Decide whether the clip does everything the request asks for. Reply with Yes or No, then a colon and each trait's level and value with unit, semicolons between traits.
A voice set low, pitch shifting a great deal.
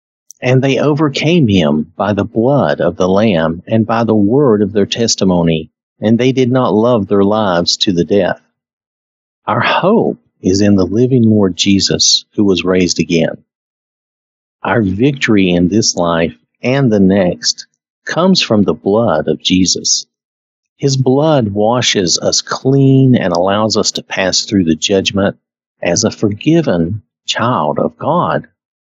Yes: low, 105 Hz; wide, 6.2 semitones